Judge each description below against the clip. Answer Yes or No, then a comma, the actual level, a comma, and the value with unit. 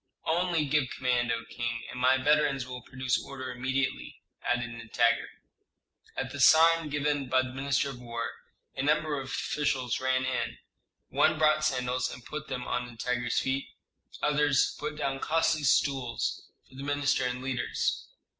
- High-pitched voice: No, low, 130 Hz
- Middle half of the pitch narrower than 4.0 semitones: Yes, average, 2.9 semitones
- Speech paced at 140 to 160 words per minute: Yes, average, 155 wpm